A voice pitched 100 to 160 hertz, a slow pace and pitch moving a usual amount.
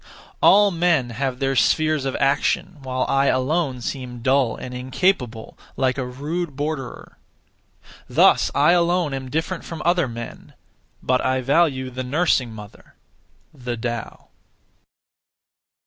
Yes: low, 135 Hz; slow, 130 wpm; average, 3.9 semitones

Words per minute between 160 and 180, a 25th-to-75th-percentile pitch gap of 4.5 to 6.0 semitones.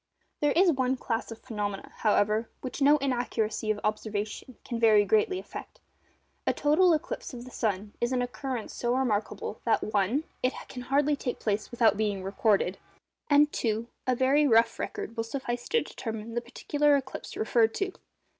No: average, 170 wpm; average, 3.7 semitones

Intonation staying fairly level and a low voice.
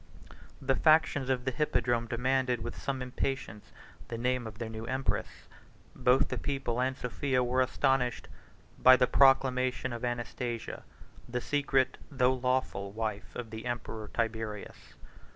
Yes: narrow, 2.1 semitones; low, 125 Hz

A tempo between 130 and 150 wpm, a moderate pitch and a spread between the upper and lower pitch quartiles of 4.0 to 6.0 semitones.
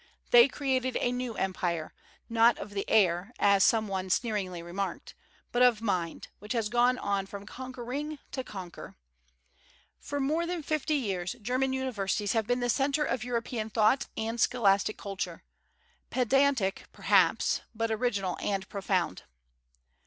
No: average, 145 wpm; high, 225 Hz; average, 4.3 semitones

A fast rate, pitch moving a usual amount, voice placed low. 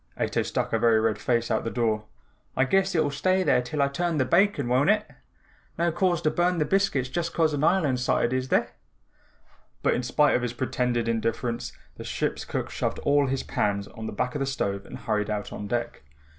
No: fast, 215 wpm; wide, 5.7 semitones; low, 130 Hz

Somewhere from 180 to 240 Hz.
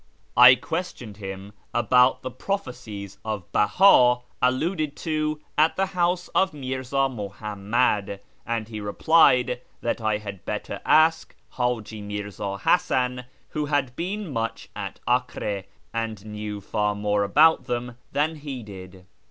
No: low, 120 Hz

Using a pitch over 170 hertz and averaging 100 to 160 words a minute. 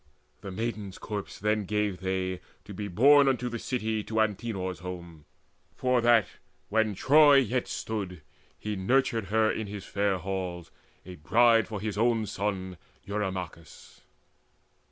No: low, 105 Hz; average, 140 wpm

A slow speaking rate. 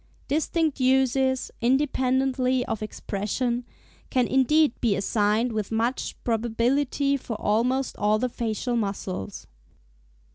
Yes: slow, 105 wpm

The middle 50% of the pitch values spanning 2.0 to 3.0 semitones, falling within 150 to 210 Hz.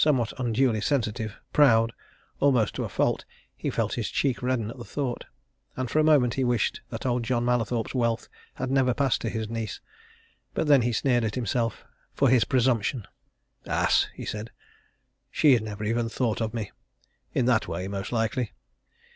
No: narrow, 2.5 semitones; low, 120 Hz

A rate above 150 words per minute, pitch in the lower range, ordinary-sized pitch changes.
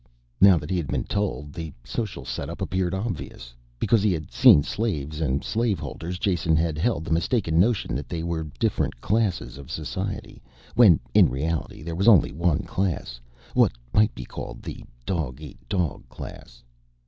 Yes: average, 170 wpm; very low, 85 Hz; average, 4.9 semitones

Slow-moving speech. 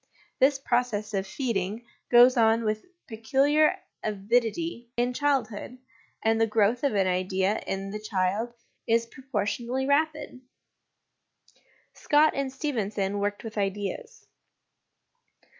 Yes: slow, 110 wpm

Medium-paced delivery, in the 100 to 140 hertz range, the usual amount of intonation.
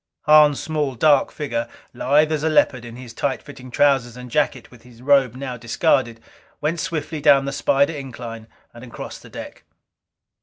Yes: average, 175 wpm; low, 135 Hz; average, 3.5 semitones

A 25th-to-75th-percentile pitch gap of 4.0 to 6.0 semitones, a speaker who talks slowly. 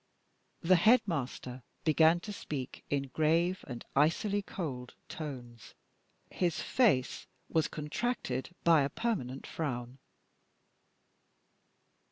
Yes: wide, 5.4 semitones; slow, 95 wpm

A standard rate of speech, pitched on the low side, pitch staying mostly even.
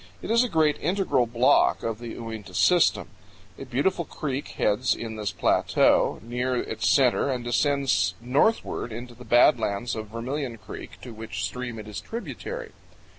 No: average, 165 wpm; low, 125 Hz; average, 4.1 semitones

